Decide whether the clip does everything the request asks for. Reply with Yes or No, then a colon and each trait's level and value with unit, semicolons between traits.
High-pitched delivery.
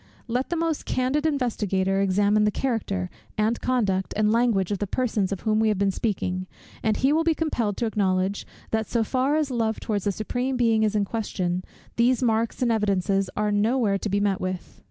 Yes: high, 215 Hz